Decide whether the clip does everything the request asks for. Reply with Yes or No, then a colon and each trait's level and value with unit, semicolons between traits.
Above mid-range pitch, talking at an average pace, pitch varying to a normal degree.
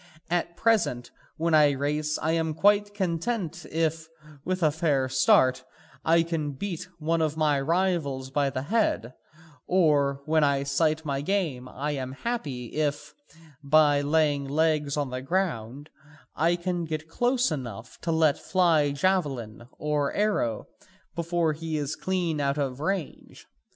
No: medium, 155 Hz; average, 145 wpm; average, 3.3 semitones